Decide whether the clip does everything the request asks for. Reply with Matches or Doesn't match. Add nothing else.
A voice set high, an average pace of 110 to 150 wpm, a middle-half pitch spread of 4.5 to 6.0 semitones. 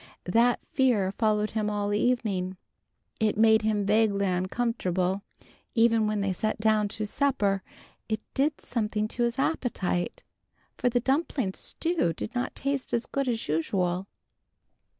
Doesn't match